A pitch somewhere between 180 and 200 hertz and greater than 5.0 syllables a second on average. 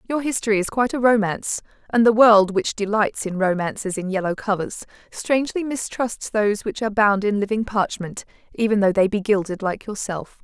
No: high, 210 Hz; 5.5 syllables/s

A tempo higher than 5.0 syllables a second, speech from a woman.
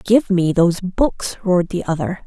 No: 4.9 syllables/s; female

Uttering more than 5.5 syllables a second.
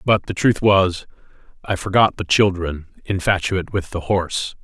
No: 4.8 syllables/s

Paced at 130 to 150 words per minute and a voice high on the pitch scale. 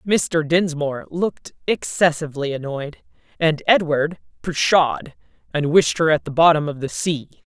No: slow, 135 wpm; medium, 160 Hz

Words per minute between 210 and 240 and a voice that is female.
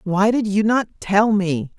No: average, 200 wpm; female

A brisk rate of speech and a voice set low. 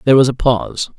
Yes: fast, 245 wpm; low, 125 Hz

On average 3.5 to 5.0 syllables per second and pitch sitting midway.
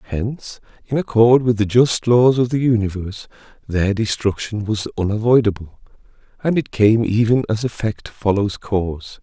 No: 4.9 syllables/s; low, 110 Hz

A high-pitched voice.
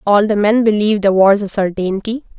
Yes: high, 205 Hz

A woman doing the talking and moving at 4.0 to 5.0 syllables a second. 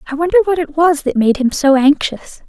No: female; 5.6 syllables/s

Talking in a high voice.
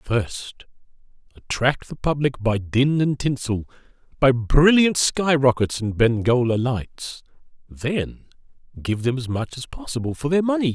No: low, 130 Hz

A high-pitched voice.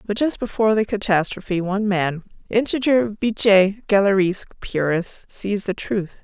Yes: high, 200 Hz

